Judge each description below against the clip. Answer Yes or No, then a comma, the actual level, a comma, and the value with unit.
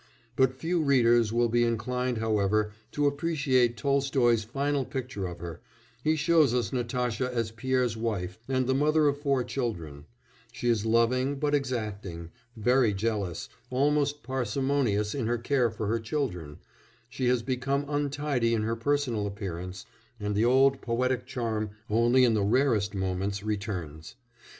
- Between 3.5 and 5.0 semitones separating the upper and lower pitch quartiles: Yes, average, 4.0 semitones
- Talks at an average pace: Yes, average, 150 wpm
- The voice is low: Yes, low, 120 Hz